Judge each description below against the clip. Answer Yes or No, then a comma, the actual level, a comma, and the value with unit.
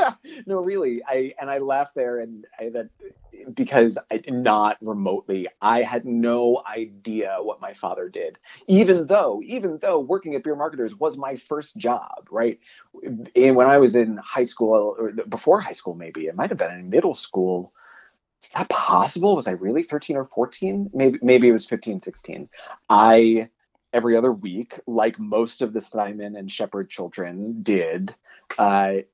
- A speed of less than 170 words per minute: No, average, 175 wpm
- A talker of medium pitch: No, low, 120 Hz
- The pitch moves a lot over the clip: Yes, wide, 6.0 semitones